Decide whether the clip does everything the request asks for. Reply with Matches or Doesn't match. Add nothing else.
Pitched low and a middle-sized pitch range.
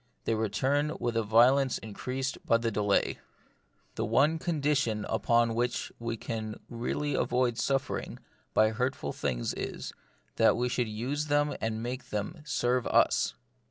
Matches